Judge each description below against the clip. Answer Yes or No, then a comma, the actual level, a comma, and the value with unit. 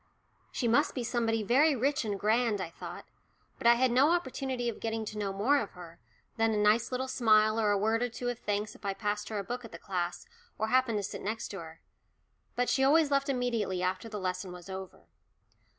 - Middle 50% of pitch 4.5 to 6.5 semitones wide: No, average, 3.4 semitones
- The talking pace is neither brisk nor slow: No, fast, 225 wpm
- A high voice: Yes, high, 225 Hz